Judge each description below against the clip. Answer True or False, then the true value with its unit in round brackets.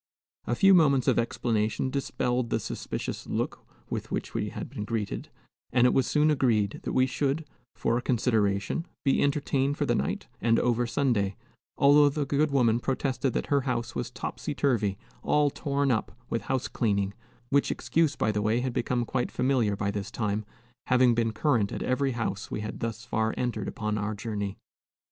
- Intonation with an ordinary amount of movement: True (4.2 semitones)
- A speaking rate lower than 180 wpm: False (185 wpm)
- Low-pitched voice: True (120 Hz)